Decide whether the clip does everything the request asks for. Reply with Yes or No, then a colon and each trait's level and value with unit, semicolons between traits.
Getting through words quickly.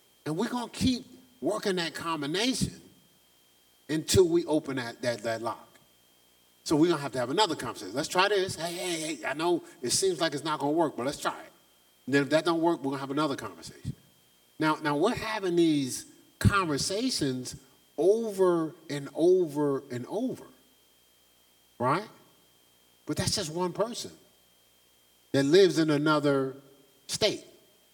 No: average, 160 wpm